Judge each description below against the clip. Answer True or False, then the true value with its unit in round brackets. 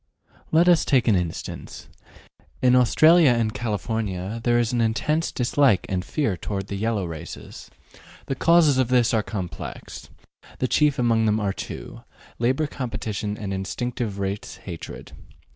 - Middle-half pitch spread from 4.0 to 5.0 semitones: True (4.4 semitones)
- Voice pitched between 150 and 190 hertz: False (115 Hz)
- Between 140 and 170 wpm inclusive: True (145 wpm)